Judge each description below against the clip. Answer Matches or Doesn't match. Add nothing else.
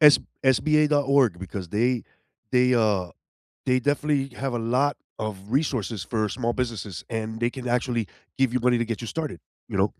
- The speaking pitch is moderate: Doesn't match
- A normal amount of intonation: Matches